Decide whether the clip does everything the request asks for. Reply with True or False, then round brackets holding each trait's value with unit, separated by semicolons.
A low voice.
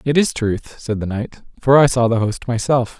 True (120 Hz)